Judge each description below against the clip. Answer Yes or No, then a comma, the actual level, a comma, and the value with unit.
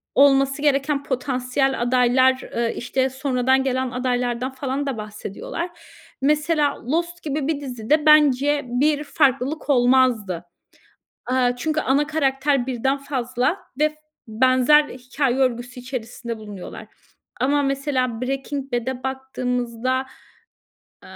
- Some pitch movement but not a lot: No, narrow, 2.3 semitones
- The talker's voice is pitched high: Yes, very high, 260 Hz